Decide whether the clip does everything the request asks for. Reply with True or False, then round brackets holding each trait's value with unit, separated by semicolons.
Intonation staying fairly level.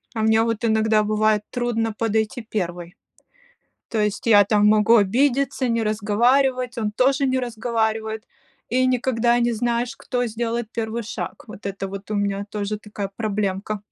True (2.2 semitones)